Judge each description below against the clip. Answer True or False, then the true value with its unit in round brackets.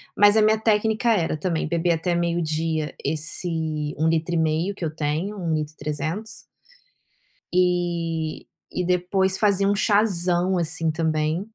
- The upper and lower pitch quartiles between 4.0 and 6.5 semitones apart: False (3.2 semitones)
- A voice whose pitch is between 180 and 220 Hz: False (170 Hz)